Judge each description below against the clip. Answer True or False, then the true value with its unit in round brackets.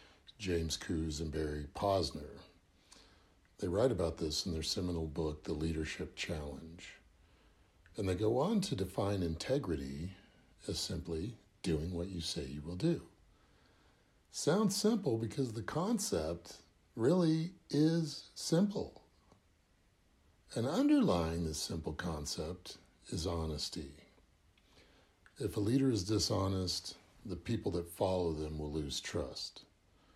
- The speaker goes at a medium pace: False (120 wpm)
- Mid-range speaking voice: False (85 Hz)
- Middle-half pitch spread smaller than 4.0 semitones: False (5.0 semitones)